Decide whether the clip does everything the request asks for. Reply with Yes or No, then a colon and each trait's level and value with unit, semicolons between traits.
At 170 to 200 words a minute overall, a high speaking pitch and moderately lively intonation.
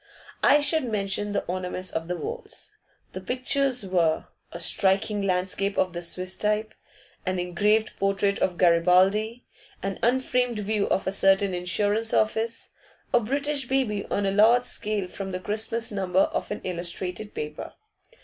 No: average, 150 wpm; high, 200 Hz; average, 3.3 semitones